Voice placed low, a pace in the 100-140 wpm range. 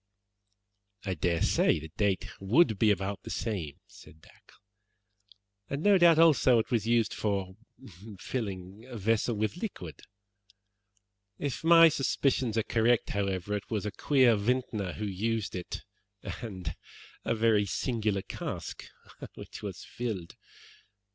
Yes: low, 110 Hz; slow, 135 wpm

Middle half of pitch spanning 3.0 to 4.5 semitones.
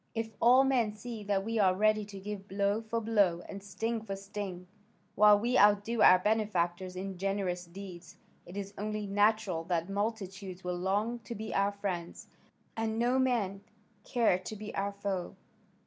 No: narrow, 2.5 semitones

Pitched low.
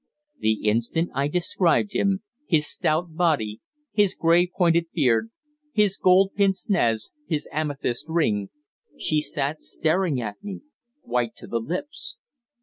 No: medium, 160 Hz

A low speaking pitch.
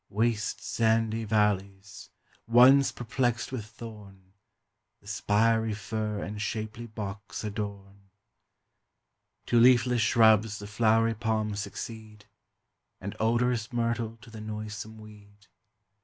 Yes: low, 110 Hz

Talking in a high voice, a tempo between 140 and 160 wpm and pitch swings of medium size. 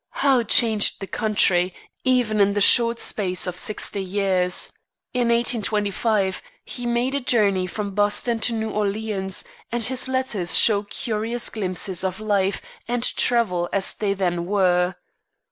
Yes: high, 210 Hz; average, 145 wpm; average, 3.5 semitones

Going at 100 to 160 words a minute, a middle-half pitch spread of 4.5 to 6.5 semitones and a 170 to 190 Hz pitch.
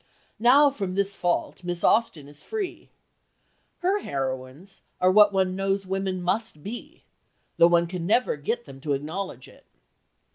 Yes: average, 150 wpm; average, 5.3 semitones; medium, 185 Hz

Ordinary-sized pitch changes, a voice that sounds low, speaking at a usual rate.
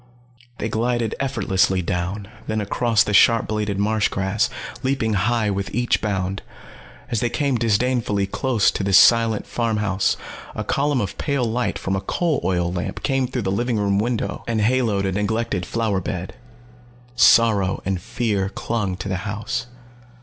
Yes: average, 3.5 semitones; low, 110 Hz; average, 165 wpm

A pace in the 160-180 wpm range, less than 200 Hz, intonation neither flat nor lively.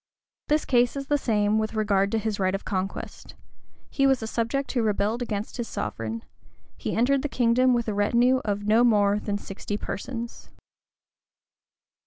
No: average, 170 wpm; high, 220 Hz; average, 3.1 semitones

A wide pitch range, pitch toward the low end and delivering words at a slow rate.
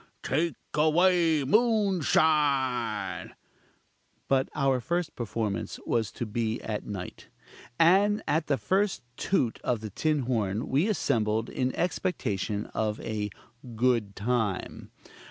Yes: wide, 6.8 semitones; low, 130 Hz; slow, 115 wpm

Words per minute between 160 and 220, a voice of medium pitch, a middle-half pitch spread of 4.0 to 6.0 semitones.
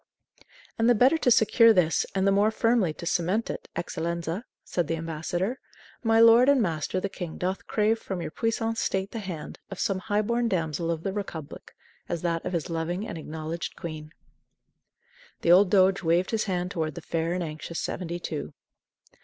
Yes: average, 185 wpm; medium, 180 Hz; average, 4.5 semitones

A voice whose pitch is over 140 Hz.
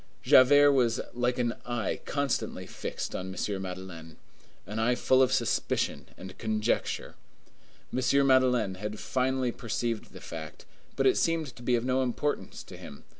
No: low, 120 Hz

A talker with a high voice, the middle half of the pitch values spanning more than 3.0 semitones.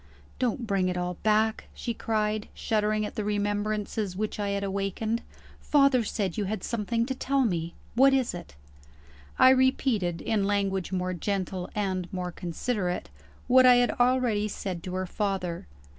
Yes: high, 210 Hz; average, 3.7 semitones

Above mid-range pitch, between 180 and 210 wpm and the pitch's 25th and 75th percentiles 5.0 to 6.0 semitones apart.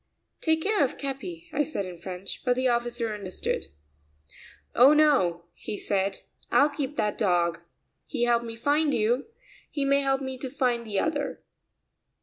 No: very high, 250 Hz; average, 165 wpm; wide, 5.4 semitones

